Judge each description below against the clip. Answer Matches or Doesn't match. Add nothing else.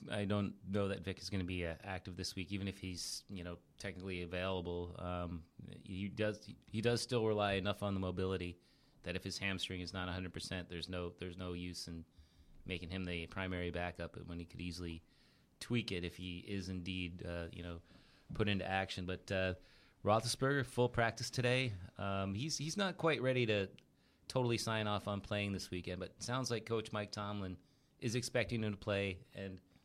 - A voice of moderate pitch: Doesn't match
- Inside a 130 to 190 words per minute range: Doesn't match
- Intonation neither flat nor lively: Matches